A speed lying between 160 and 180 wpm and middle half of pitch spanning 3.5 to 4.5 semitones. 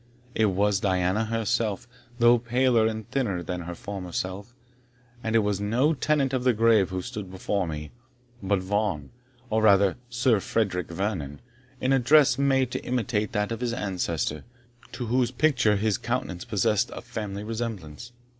Yes: average, 165 wpm; average, 4.0 semitones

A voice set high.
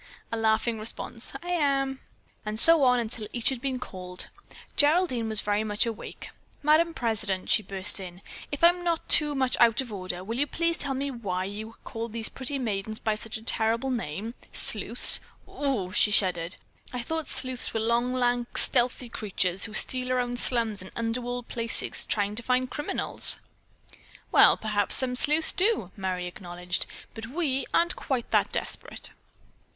Yes: high, 235 Hz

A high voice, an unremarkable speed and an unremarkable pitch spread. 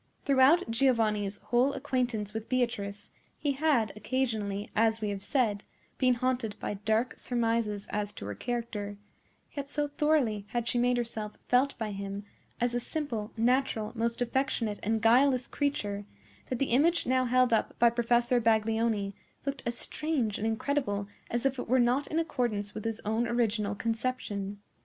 Yes: high, 235 Hz; average, 160 wpm; average, 3.3 semitones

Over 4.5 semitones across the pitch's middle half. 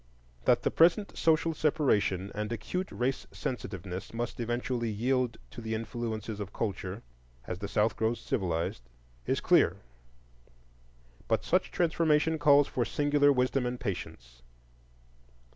Yes: wide, 5.5 semitones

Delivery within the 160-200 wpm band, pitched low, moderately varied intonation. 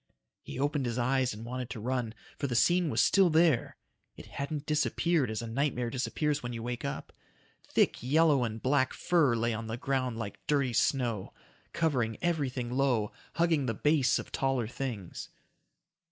Yes: average, 170 wpm; low, 130 Hz; average, 3.9 semitones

